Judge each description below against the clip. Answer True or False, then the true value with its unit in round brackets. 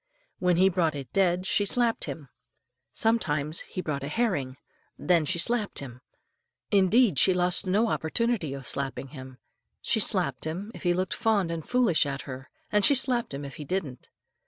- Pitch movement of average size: False (6.6 semitones)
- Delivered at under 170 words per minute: False (180 wpm)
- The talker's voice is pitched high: False (175 Hz)